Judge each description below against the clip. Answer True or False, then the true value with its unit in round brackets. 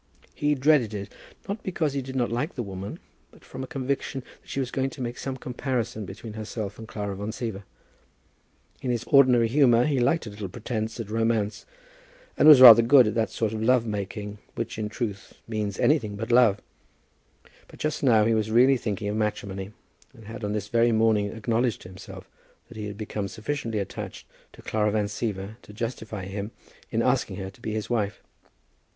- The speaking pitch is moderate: False (110 Hz)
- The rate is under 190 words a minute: False (195 wpm)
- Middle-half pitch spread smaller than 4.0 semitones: True (3.1 semitones)